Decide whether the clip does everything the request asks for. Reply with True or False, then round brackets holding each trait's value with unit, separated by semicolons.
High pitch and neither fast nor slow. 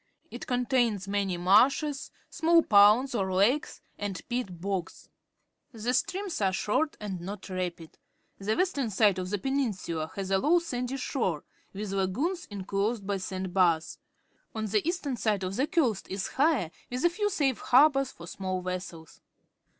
True (205 Hz; 160 wpm)